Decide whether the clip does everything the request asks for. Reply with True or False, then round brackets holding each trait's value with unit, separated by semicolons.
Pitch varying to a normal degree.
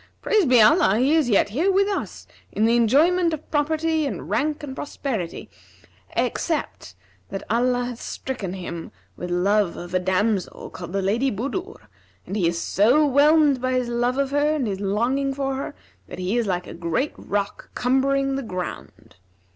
False (6.3 semitones)